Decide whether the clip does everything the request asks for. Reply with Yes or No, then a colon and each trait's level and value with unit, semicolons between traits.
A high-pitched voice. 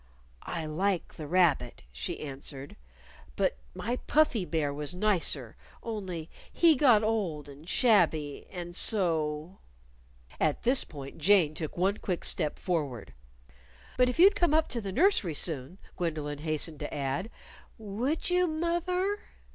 No: medium, 175 Hz